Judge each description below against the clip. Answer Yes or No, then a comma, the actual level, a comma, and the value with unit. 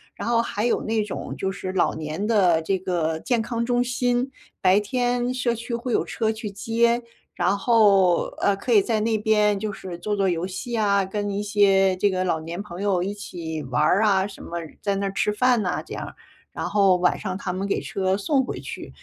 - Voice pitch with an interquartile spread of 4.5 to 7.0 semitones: No, average, 3.4 semitones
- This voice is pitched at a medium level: No, high, 205 Hz